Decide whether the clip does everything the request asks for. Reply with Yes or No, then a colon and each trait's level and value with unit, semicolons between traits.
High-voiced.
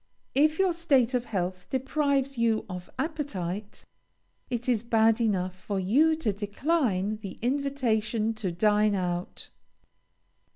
Yes: high, 225 Hz